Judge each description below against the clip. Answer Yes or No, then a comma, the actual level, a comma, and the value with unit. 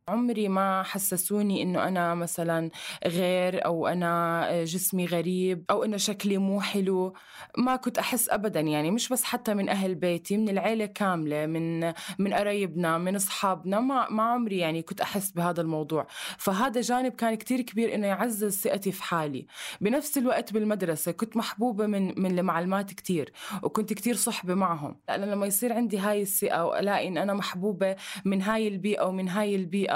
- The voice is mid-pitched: No, high, 195 Hz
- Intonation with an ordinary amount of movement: Yes, average, 3.1 semitones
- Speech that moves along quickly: Yes, fast, 165 wpm